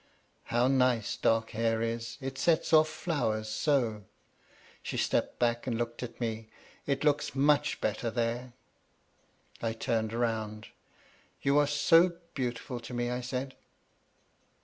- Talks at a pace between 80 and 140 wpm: Yes, slow, 135 wpm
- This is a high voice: No, low, 120 Hz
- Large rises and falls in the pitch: No, average, 3.3 semitones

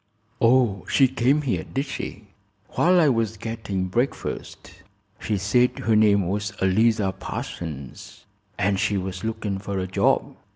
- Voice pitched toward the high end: No, low, 105 Hz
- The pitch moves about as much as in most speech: Yes, average, 3.7 semitones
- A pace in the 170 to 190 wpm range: No, average, 140 wpm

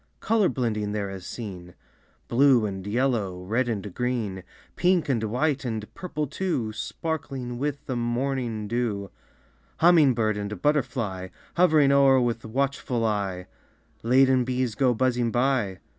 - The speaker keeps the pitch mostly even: No, average, 4.3 semitones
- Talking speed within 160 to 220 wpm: No, slow, 135 wpm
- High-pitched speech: No, low, 120 Hz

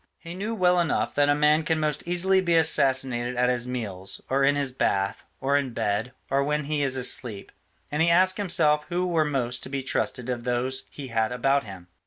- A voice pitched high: No, medium, 140 Hz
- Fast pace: Yes, fast, 215 wpm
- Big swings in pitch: No, average, 4.3 semitones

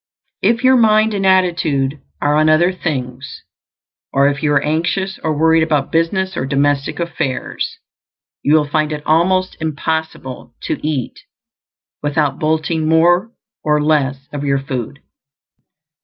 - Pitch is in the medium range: Yes, medium, 155 Hz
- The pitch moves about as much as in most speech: Yes, average, 3.4 semitones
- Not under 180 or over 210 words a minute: No, average, 140 wpm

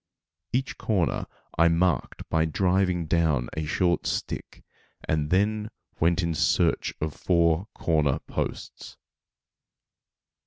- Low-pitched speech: Yes, very low, 85 Hz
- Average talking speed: No, slow, 110 wpm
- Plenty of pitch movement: No, average, 2.8 semitones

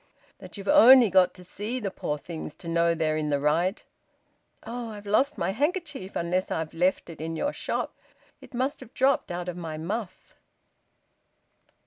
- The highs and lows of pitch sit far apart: Yes, wide, 5.9 semitones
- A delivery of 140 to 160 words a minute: No, average, 175 wpm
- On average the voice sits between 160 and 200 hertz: Yes, medium, 185 Hz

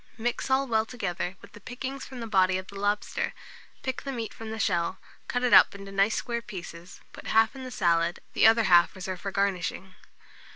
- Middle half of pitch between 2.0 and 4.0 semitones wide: No, average, 4.4 semitones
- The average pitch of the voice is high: Yes, high, 205 Hz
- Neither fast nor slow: No, fast, 210 wpm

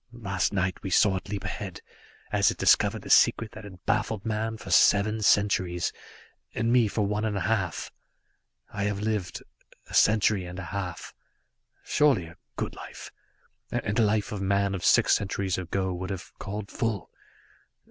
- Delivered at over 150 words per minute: Yes, average, 170 wpm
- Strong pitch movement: No, narrow, 2.4 semitones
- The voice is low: Yes, low, 100 Hz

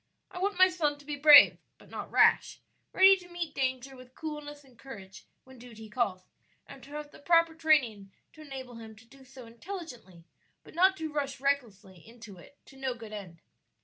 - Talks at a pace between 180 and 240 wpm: Yes, average, 195 wpm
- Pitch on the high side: Yes, very high, 270 Hz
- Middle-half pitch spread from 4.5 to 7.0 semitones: Yes, average, 5.1 semitones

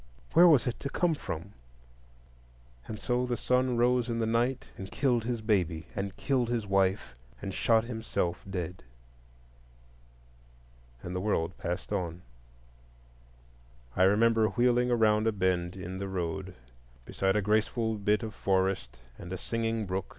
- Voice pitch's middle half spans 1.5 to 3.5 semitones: No, average, 4.1 semitones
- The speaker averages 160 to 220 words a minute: No, average, 150 wpm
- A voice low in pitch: Yes, low, 105 Hz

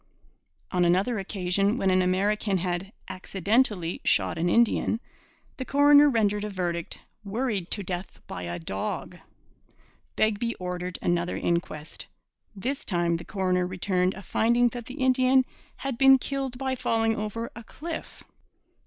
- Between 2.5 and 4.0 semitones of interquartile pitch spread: No, average, 5.0 semitones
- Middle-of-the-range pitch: No, high, 200 Hz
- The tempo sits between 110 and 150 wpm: Yes, average, 140 wpm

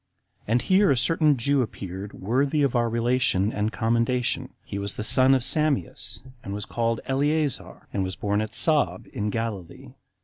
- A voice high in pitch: No, low, 115 Hz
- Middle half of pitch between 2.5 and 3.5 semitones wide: No, average, 4.8 semitones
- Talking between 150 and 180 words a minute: Yes, average, 170 wpm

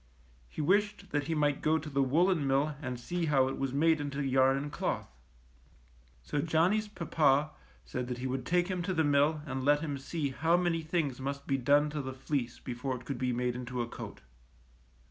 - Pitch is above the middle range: No, medium, 145 Hz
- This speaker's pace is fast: Yes, fast, 210 wpm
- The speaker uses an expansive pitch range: No, average, 3.4 semitones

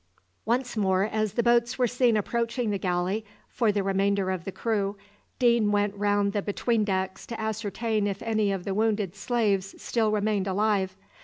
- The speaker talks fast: No, average, 175 wpm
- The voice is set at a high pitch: Yes, high, 210 Hz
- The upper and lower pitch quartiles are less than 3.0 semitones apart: Yes, narrow, 2.4 semitones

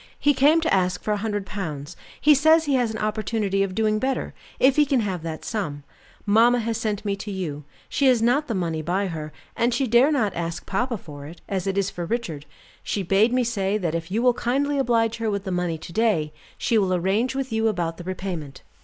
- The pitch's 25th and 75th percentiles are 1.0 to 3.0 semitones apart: No, average, 5.0 semitones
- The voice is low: No, high, 205 Hz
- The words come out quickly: Yes, fast, 235 wpm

